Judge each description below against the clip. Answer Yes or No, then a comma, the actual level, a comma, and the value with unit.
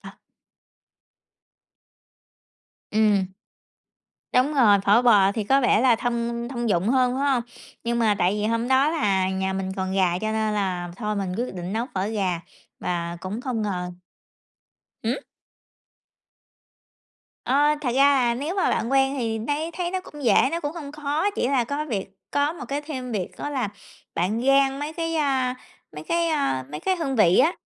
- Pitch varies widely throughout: Yes, wide, 5.8 semitones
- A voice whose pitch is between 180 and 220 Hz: No, high, 235 Hz